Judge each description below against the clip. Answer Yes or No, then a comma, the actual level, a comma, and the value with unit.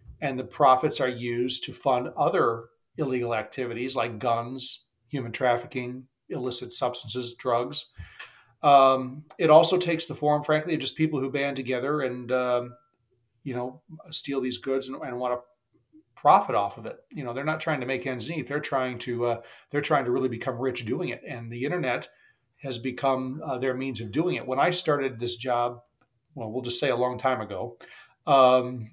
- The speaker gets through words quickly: No, average, 190 wpm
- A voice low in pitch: Yes, low, 130 Hz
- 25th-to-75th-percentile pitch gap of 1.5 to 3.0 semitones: Yes, narrow, 2.4 semitones